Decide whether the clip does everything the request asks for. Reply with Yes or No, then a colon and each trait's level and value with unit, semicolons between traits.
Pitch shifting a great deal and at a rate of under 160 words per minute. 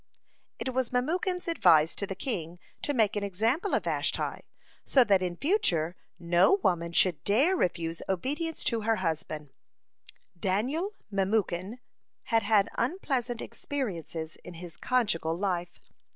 Yes: wide, 7.0 semitones; slow, 135 wpm